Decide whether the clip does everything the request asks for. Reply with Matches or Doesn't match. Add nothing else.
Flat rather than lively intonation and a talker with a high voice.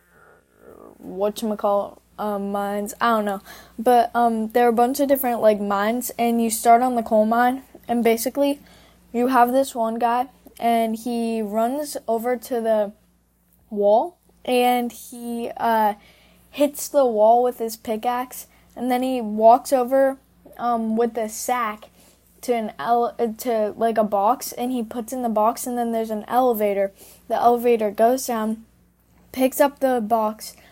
Matches